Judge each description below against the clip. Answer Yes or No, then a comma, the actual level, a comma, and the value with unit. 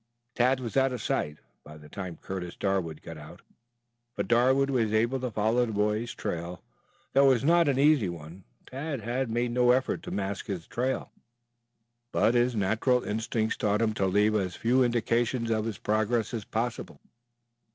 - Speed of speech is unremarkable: Yes, average, 180 wpm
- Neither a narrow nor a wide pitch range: Yes, average, 3.8 semitones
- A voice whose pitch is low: Yes, low, 115 Hz